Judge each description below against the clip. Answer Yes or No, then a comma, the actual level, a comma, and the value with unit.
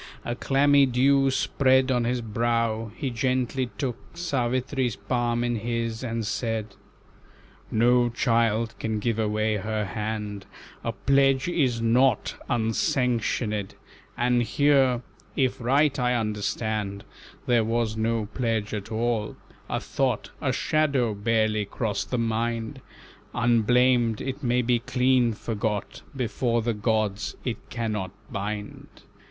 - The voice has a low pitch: Yes, low, 115 Hz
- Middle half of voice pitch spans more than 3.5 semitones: No, narrow, 2.5 semitones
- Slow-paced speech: Yes, slow, 125 wpm